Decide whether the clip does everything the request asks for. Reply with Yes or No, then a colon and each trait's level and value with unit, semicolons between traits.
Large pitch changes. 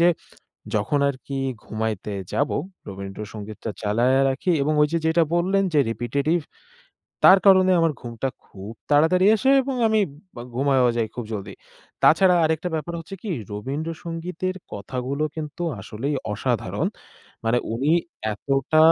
Yes: wide, 6.6 semitones